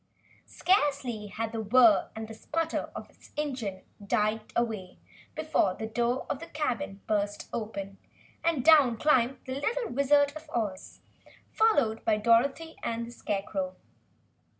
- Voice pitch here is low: No, high, 235 Hz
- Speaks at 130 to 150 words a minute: Yes, slow, 135 wpm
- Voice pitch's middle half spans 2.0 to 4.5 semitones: No, average, 5.3 semitones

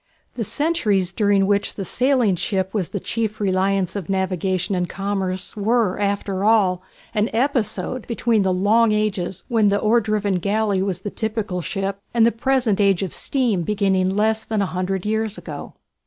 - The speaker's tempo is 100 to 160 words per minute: No, average, 170 wpm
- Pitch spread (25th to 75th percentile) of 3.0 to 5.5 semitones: No, narrow, 2.5 semitones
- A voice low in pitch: No, high, 200 Hz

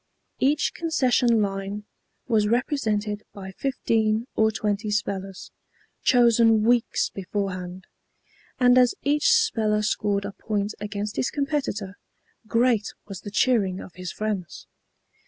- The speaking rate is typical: No, slow, 120 wpm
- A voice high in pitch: Yes, high, 215 Hz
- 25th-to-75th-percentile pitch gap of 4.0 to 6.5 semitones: No, average, 3.4 semitones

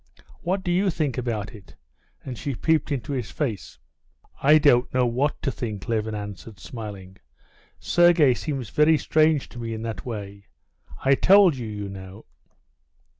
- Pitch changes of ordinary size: No, wide, 6.1 semitones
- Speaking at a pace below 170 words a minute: Yes, average, 160 wpm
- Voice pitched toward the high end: No, low, 125 Hz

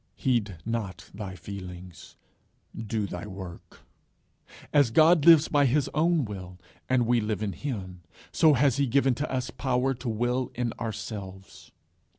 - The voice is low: Yes, low, 115 Hz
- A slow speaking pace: No, average, 150 wpm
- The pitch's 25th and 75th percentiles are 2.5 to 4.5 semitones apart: No, wide, 5.4 semitones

